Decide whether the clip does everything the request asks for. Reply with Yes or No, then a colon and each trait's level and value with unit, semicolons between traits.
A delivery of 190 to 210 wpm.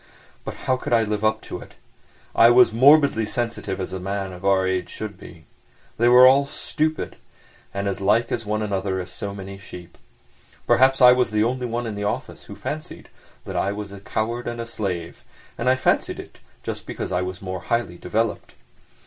Yes: average, 200 wpm